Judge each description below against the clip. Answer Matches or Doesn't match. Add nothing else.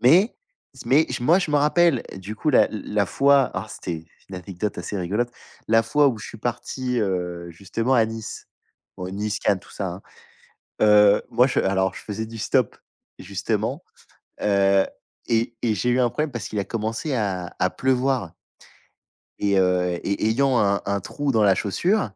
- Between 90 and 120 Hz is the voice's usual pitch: Matches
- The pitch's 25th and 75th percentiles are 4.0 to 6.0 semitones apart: Matches